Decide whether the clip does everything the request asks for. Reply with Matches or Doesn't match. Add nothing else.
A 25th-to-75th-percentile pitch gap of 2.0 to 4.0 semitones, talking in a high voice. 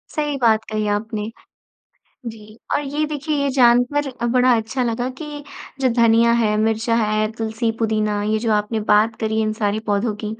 Matches